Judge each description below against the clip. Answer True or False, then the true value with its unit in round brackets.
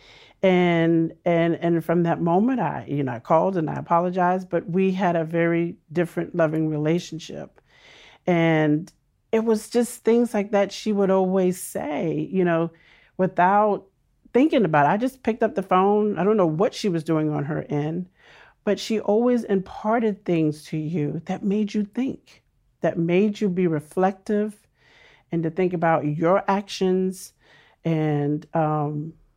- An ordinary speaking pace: True (160 wpm)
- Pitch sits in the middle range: True (180 Hz)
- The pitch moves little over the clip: False (3.8 semitones)